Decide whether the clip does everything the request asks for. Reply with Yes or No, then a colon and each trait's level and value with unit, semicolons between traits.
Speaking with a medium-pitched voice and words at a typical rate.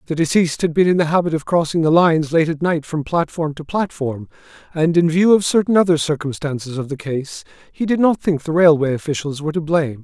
No: medium, 160 Hz; fast, 225 wpm